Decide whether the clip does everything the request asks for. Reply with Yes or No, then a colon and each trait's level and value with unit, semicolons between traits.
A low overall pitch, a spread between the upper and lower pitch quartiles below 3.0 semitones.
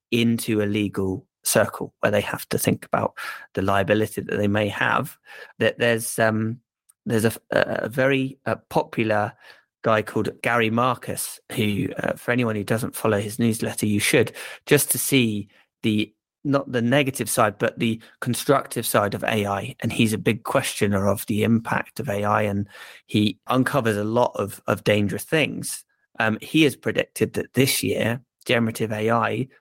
Yes: low, 115 Hz; narrow, 2.4 semitones